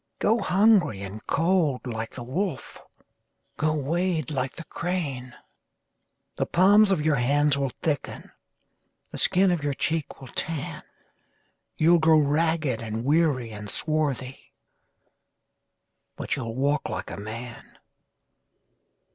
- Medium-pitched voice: Yes, medium, 150 Hz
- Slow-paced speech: Yes, slow, 115 wpm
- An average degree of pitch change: Yes, average, 4.7 semitones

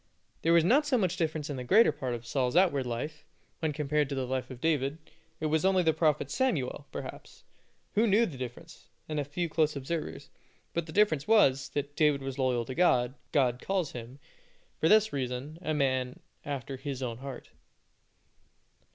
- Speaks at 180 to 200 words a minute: Yes, average, 190 wpm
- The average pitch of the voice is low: No, medium, 145 Hz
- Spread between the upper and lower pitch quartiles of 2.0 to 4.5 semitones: Yes, average, 4.1 semitones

